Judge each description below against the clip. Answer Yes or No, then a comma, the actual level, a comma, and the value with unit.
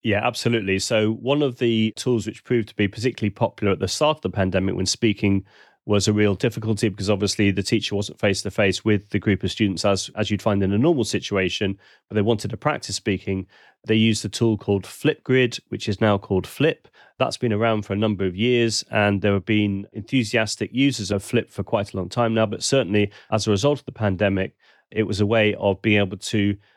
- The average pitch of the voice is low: Yes, low, 105 Hz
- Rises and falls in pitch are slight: Yes, narrow, 2.3 semitones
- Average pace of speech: No, fast, 225 wpm